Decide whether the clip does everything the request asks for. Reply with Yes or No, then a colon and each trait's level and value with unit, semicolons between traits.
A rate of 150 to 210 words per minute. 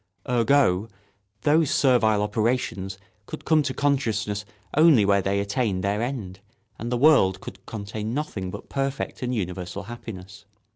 No: average, 140 wpm